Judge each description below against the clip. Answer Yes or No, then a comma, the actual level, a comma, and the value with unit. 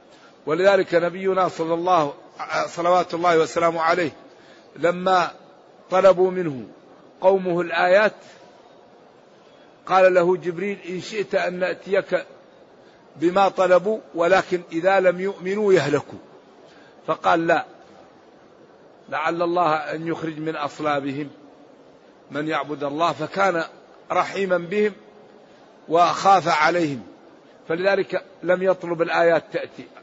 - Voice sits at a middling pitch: Yes, medium, 175 Hz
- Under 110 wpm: Yes, average, 95 wpm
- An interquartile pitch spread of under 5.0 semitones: Yes, narrow, 2.4 semitones